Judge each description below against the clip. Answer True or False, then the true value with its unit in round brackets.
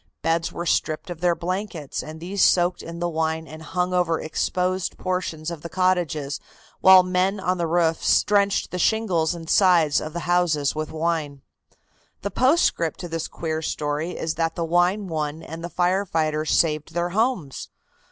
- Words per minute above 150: True (170 wpm)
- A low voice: False (170 Hz)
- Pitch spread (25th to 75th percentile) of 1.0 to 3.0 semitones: True (2.4 semitones)